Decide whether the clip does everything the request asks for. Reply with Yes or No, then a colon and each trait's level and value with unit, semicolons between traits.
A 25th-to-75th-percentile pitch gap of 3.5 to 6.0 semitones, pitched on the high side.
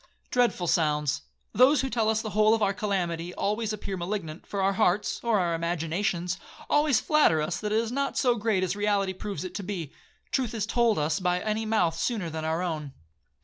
Yes: average, 4.3 semitones; high, 195 Hz